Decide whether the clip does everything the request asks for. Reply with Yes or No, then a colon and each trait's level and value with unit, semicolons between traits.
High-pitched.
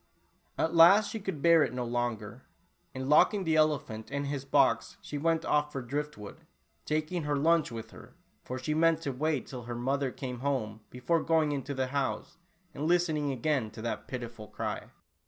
No: medium, 140 Hz